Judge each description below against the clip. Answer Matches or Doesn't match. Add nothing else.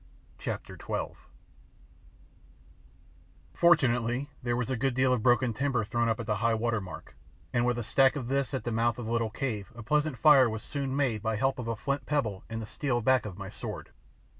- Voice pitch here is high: Doesn't match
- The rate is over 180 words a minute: Matches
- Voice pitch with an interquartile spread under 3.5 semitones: Matches